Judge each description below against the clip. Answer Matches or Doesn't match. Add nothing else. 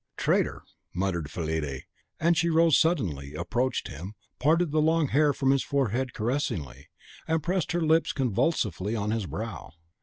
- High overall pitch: Doesn't match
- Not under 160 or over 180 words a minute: Doesn't match